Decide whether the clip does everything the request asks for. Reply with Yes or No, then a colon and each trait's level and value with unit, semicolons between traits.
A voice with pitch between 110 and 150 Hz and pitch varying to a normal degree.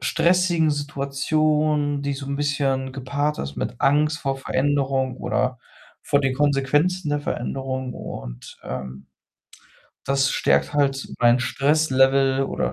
No: medium, 140 Hz; narrow, 1.8 semitones